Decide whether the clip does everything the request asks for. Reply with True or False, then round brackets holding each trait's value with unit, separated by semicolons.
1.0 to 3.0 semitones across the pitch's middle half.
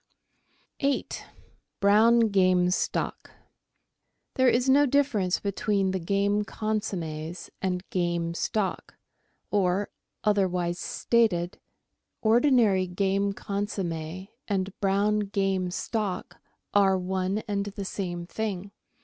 True (2.6 semitones)